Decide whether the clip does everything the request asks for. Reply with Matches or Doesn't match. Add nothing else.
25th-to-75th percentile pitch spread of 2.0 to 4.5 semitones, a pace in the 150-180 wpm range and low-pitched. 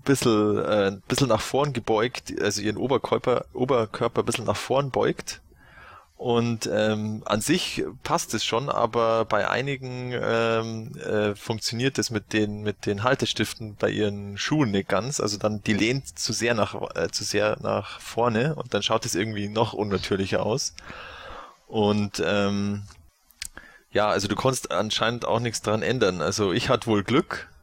Matches